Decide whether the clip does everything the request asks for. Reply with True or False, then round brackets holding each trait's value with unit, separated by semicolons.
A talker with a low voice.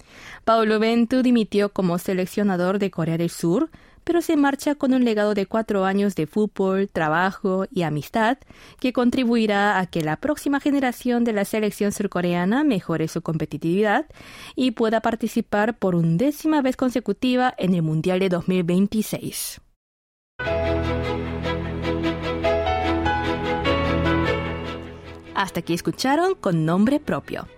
False (190 Hz)